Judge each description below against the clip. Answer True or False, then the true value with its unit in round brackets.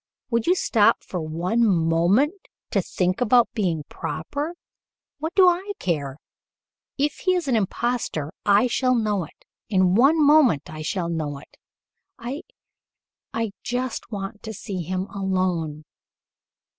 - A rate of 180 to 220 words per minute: False (140 wpm)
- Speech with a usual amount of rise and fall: False (6.9 semitones)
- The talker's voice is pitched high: True (205 Hz)